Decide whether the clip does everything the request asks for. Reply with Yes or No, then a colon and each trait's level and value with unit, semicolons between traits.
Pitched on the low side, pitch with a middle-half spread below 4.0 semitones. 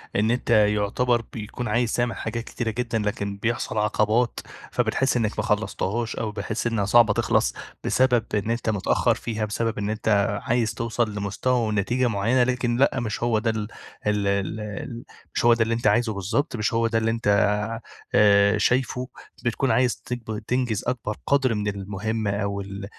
Yes: low, 110 Hz; narrow, 2.5 semitones